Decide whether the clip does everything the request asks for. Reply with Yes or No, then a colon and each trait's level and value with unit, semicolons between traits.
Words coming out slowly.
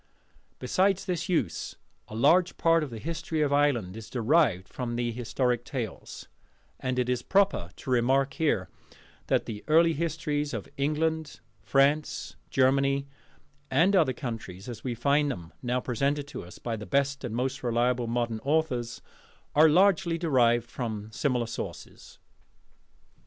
No: average, 145 wpm